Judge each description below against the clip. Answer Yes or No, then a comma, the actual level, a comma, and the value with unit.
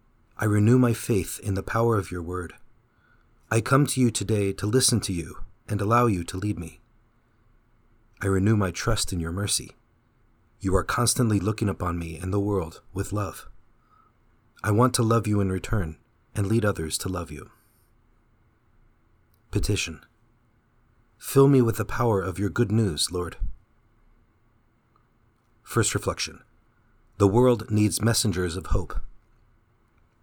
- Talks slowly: No, average, 150 wpm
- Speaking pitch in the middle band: No, low, 110 Hz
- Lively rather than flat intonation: No, average, 3.2 semitones